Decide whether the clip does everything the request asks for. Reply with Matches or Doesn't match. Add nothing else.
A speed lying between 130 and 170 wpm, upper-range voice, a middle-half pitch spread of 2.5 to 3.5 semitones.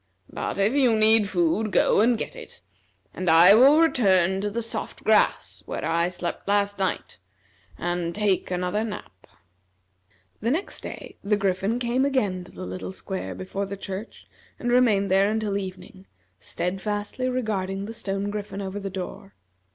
Matches